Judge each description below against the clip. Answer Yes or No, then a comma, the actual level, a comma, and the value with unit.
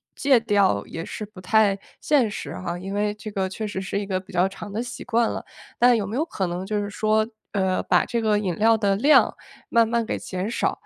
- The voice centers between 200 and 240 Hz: Yes, high, 210 Hz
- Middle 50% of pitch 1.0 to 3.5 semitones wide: Yes, average, 2.8 semitones